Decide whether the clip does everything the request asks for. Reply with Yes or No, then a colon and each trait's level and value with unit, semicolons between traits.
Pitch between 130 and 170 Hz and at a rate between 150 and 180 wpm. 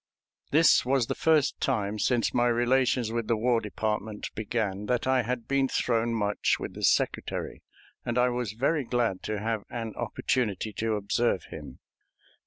No: low, 115 Hz; average, 165 wpm